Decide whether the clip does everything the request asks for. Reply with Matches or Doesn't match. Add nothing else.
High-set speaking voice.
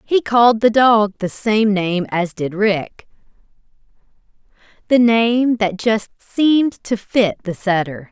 Matches